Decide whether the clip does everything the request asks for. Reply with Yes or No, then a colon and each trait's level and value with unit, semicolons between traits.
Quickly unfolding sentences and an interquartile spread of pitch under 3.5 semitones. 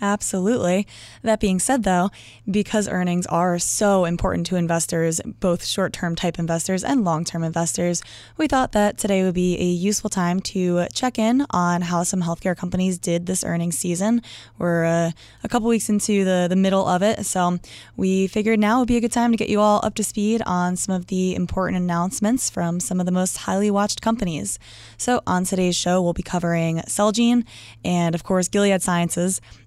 No: average, 190 wpm; average, 3.1 semitones